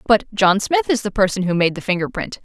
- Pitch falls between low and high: No, high, 205 Hz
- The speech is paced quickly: Yes, fast, 270 wpm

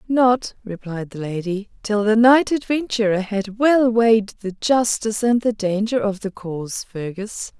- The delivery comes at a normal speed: Yes, average, 160 wpm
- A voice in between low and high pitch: No, high, 215 Hz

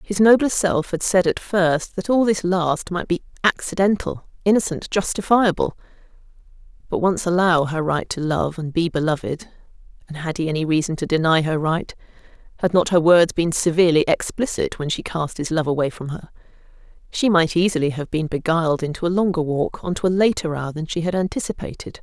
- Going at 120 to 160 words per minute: No, average, 185 wpm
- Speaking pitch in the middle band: Yes, medium, 170 Hz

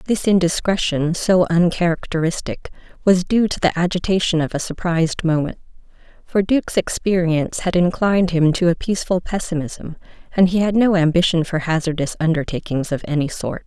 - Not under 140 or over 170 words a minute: Yes, average, 150 wpm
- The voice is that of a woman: Yes, female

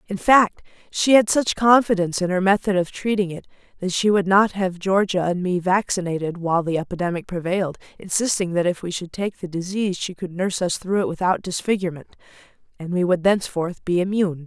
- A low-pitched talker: No, medium, 185 Hz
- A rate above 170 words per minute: Yes, average, 195 wpm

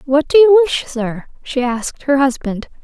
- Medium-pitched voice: No, very high, 275 Hz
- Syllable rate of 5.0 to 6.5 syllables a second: Yes, 5.3 syllables/s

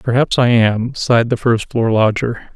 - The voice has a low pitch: Yes, low, 115 Hz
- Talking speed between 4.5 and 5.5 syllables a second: Yes, 4.6 syllables/s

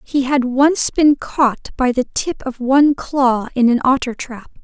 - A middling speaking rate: Yes, average, 195 wpm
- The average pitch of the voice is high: Yes, very high, 260 Hz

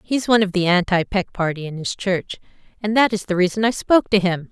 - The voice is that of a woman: Yes, female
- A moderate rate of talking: No, fast, 255 wpm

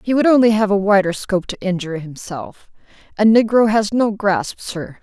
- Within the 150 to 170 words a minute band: No, average, 190 wpm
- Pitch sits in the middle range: No, high, 200 Hz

